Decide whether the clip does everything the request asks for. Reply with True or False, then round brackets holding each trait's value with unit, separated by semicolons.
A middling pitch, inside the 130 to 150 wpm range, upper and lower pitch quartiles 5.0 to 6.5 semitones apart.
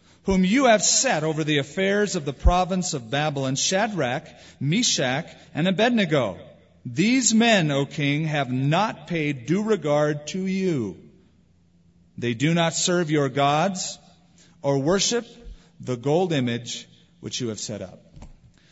True (155 Hz; 140 wpm; 5.5 semitones)